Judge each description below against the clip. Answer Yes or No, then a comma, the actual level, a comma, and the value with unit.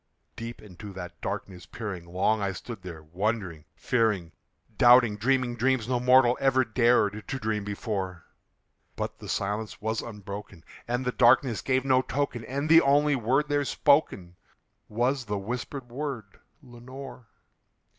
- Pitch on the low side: Yes, low, 115 Hz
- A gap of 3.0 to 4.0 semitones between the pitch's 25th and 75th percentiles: No, average, 4.4 semitones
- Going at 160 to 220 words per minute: No, average, 145 wpm